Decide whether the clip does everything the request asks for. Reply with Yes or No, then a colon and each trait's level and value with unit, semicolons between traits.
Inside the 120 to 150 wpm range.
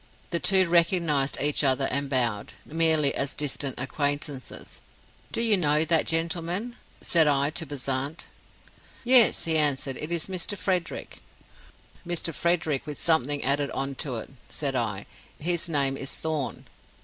Yes: average, 145 wpm